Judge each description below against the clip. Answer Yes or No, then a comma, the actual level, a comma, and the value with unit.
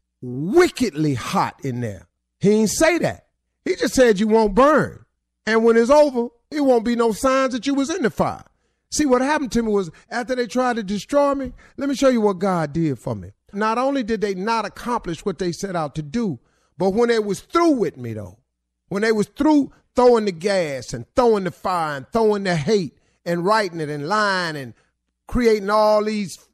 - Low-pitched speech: No, high, 215 Hz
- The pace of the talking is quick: Yes, fast, 215 wpm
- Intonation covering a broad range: Yes, wide, 7.2 semitones